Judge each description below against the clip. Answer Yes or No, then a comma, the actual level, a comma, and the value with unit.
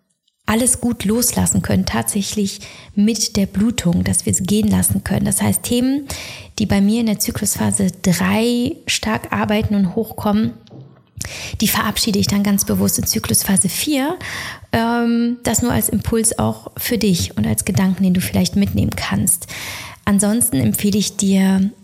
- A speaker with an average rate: Yes, average, 155 wpm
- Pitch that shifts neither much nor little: No, wide, 8.8 semitones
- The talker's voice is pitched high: Yes, high, 200 Hz